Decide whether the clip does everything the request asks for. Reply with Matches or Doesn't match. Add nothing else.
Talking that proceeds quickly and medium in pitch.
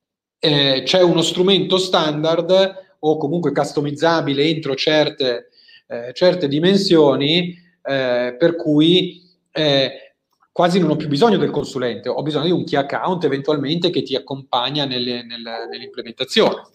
Doesn't match